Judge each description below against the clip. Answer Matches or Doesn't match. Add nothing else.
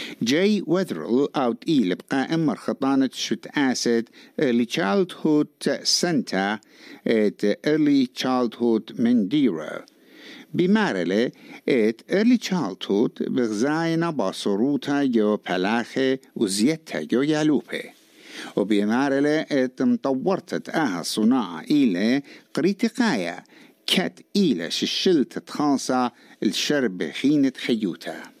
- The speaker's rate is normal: Doesn't match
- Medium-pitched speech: Matches